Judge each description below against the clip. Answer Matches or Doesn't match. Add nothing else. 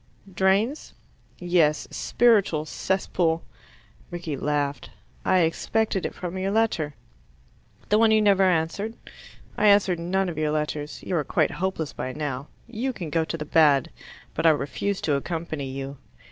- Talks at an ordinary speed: Matches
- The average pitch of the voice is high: Doesn't match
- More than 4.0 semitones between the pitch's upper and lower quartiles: Matches